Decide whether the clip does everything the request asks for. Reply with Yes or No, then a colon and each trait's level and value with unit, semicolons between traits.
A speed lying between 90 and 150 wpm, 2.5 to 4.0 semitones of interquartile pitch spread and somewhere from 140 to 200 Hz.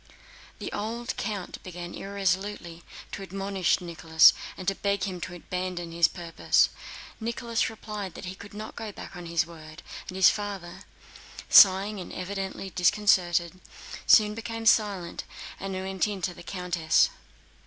Yes: average, 145 wpm; average, 2.8 semitones; high, 190 Hz